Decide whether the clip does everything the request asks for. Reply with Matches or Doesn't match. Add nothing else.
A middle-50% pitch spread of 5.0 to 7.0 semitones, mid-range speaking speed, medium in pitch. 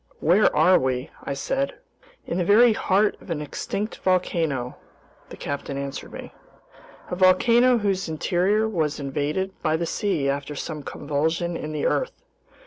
Matches